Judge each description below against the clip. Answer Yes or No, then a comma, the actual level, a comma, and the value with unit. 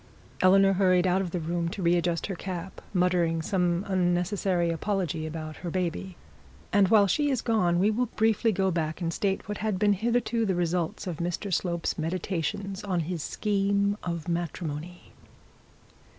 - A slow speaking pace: No, average, 165 wpm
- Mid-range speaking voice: Yes, medium, 180 Hz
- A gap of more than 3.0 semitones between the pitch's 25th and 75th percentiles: No, average, 2.7 semitones